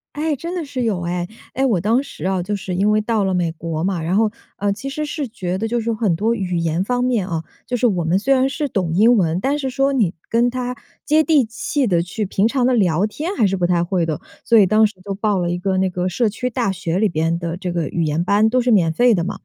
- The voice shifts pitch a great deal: Yes, wide, 5.7 semitones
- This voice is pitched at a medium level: No, high, 205 Hz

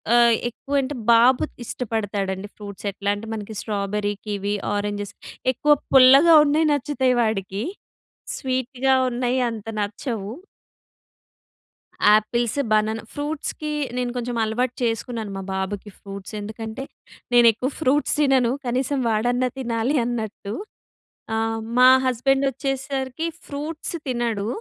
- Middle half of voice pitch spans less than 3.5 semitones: No, average, 3.9 semitones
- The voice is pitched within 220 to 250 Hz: Yes, high, 240 Hz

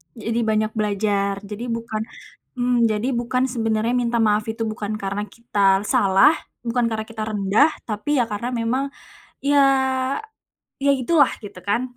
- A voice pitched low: No, high, 225 Hz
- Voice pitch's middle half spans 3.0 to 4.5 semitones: No, narrow, 2.6 semitones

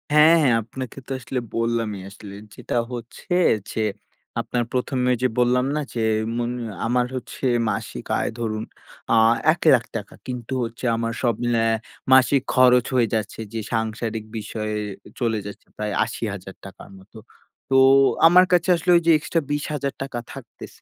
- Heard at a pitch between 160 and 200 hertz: No, low, 120 Hz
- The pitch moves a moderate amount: Yes, average, 3.0 semitones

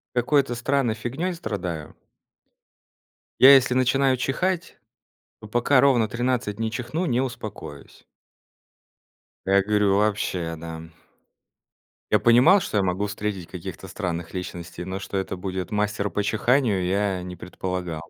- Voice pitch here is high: No, low, 105 Hz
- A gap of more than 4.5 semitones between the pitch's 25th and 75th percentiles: Yes, average, 5.2 semitones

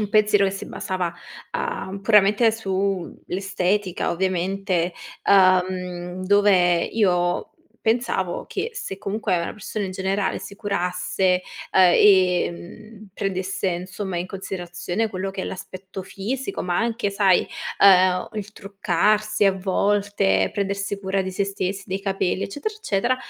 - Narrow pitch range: Yes, narrow, 1.9 semitones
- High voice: Yes, high, 195 Hz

